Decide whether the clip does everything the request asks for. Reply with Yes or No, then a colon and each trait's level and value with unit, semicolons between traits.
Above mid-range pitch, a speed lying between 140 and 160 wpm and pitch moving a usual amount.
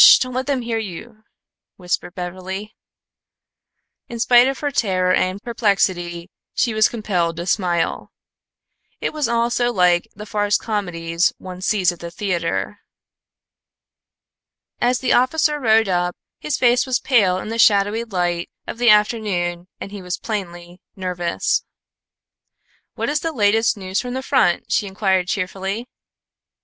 Yes: high, 205 Hz; average, 145 wpm; average, 4.6 semitones